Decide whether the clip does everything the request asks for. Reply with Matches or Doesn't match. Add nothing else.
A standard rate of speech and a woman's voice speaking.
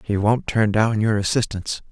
Doesn't match